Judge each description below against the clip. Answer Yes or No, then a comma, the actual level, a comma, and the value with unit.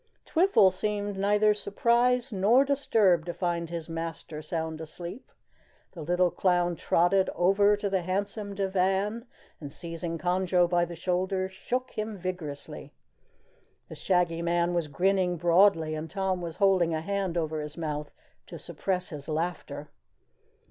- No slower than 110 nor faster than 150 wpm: Yes, average, 140 wpm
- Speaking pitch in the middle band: Yes, medium, 180 Hz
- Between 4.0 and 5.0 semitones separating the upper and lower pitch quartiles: No, average, 3.0 semitones